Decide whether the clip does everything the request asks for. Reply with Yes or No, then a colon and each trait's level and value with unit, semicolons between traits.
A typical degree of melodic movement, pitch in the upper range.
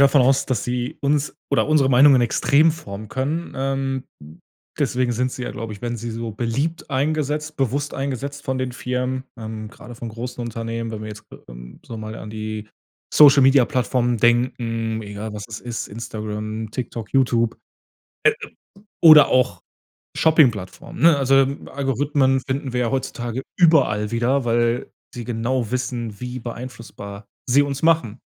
No: average, 3.3 semitones; low, 125 Hz